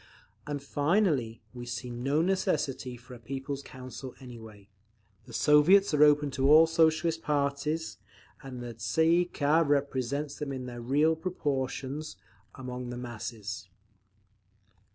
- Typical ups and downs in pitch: Yes, average, 3.6 semitones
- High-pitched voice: No, medium, 140 Hz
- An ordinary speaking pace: No, slow, 130 wpm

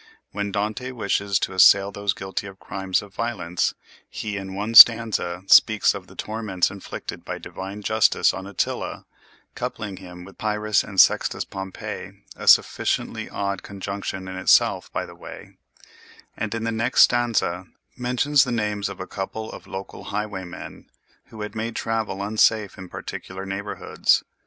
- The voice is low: Yes, low, 100 Hz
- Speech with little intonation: Yes, narrow, 2.3 semitones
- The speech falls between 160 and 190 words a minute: No, average, 150 wpm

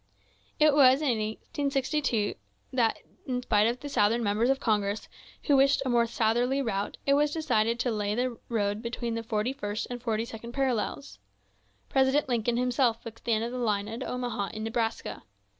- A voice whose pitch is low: No, high, 235 Hz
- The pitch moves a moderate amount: Yes, average, 3.0 semitones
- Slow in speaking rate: No, average, 180 wpm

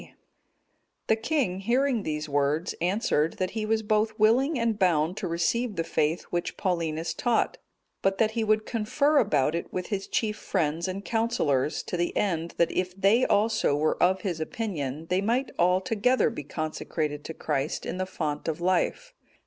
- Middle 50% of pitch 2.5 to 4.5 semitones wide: No, wide, 5.4 semitones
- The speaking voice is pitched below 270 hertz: Yes, medium, 185 Hz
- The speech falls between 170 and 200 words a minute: Yes, average, 180 wpm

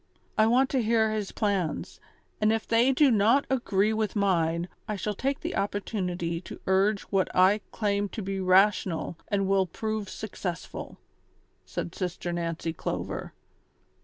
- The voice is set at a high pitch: Yes, high, 200 Hz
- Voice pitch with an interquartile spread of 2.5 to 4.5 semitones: Yes, average, 2.9 semitones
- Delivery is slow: No, average, 150 wpm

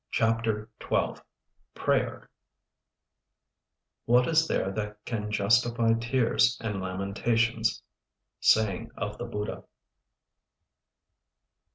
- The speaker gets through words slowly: Yes, slow, 80 wpm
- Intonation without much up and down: Yes, narrow, 2.0 semitones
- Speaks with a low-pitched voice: Yes, low, 110 Hz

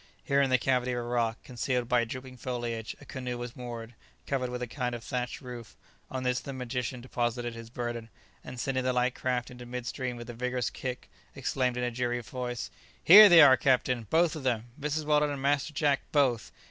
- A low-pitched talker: Yes, low, 125 Hz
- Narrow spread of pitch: Yes, narrow, 1.5 semitones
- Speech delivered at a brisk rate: Yes, fast, 210 wpm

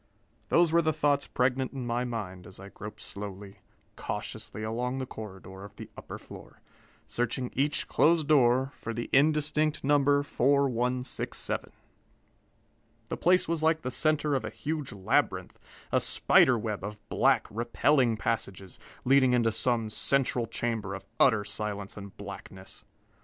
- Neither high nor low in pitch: No, low, 120 Hz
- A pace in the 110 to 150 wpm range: Yes, average, 145 wpm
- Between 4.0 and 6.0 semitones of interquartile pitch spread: Yes, average, 4.9 semitones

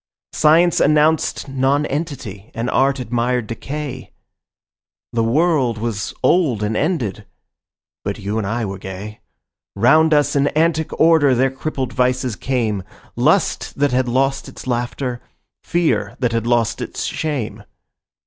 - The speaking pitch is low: Yes, low, 130 Hz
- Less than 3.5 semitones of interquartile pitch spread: No, average, 4.4 semitones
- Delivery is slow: Yes, slow, 130 wpm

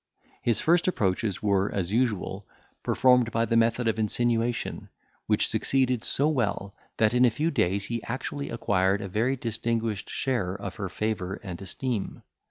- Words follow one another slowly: No, average, 160 wpm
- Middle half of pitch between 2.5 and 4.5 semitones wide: Yes, average, 3.7 semitones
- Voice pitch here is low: Yes, low, 115 Hz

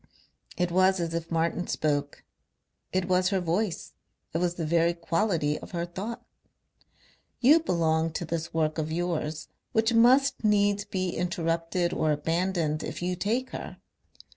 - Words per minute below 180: Yes, average, 150 wpm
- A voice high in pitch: No, medium, 175 Hz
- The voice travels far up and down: No, average, 2.8 semitones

